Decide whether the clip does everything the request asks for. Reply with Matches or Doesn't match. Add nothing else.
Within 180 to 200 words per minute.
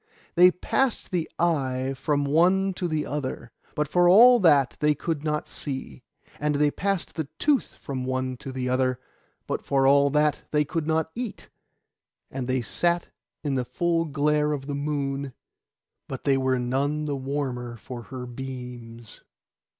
Doesn't match